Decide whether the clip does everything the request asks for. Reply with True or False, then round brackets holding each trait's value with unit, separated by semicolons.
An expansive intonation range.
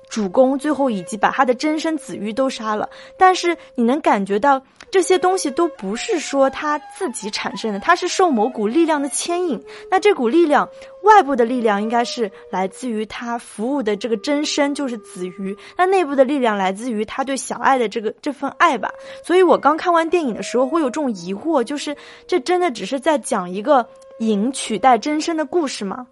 True (5.7 semitones)